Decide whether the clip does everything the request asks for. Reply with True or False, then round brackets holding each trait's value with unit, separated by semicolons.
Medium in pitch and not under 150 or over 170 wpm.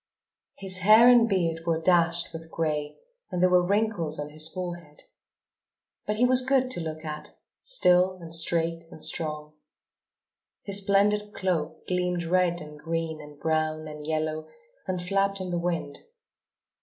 True (170 Hz; 155 wpm)